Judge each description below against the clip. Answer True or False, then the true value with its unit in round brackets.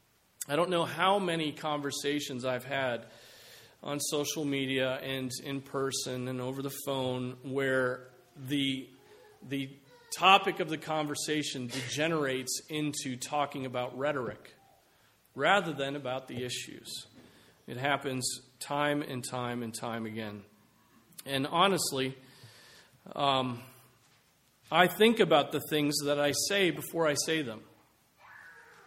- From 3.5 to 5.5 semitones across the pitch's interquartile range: False (2.7 semitones)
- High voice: False (140 Hz)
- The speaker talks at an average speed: False (120 wpm)